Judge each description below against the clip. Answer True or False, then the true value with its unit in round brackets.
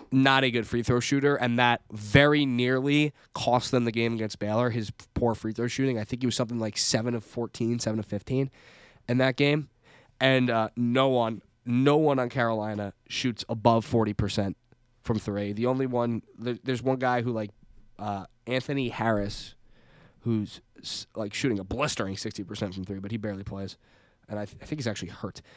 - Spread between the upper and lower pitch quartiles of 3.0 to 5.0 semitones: True (3.3 semitones)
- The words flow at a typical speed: True (190 wpm)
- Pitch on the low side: True (120 Hz)